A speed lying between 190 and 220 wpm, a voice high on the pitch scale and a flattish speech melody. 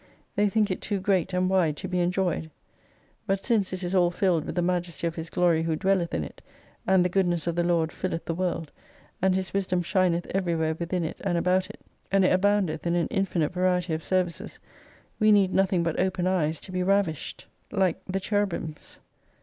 No: fast, 205 wpm; medium, 180 Hz; narrow, 2.0 semitones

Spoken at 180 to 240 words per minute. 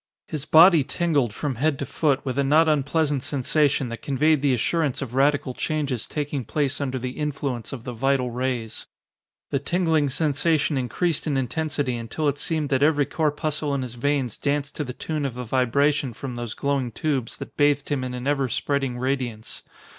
Yes: average, 185 wpm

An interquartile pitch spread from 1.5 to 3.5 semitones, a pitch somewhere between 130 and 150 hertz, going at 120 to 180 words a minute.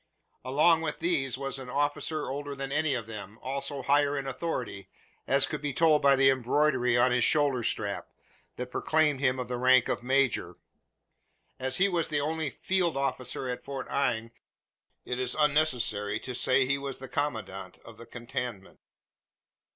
Yes: average, 2.9 semitones; low, 135 Hz; average, 170 wpm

